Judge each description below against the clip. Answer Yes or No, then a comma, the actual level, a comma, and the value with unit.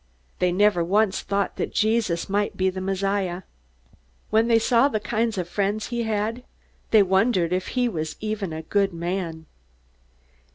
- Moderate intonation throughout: Yes, average, 3.2 semitones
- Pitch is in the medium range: No, high, 200 Hz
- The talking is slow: No, average, 160 wpm